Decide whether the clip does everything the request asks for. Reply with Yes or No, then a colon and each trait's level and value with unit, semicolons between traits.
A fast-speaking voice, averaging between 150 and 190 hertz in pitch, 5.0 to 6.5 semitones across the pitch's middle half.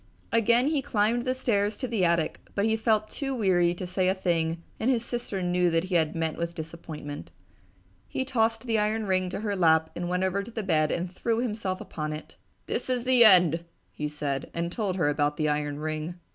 Yes: fast, 215 wpm; medium, 185 Hz; wide, 5.4 semitones